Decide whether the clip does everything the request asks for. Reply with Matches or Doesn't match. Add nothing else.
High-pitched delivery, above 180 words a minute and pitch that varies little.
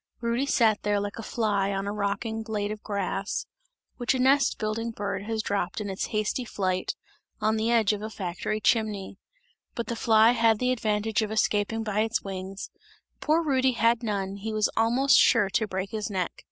Matches